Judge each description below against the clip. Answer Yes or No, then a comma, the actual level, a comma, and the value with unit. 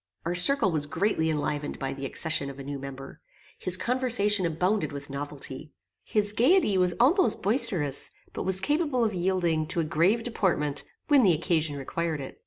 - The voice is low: No, medium, 175 Hz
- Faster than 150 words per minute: Yes, average, 175 wpm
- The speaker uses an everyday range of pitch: No, wide, 6.2 semitones